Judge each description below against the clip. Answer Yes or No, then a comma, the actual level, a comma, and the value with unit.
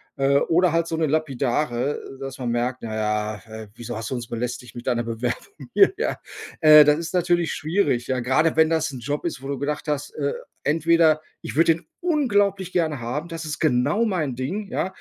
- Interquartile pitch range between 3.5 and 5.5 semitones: Yes, average, 5.2 semitones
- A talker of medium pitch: Yes, medium, 150 Hz